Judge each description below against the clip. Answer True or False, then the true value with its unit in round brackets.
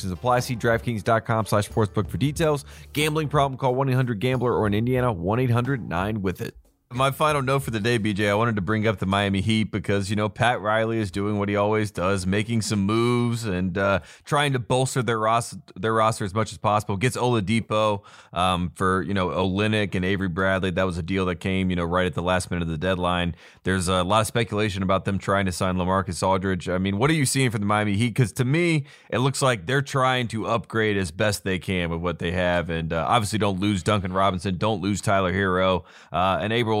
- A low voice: True (105 Hz)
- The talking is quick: True (225 wpm)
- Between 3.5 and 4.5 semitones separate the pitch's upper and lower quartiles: True (4.0 semitones)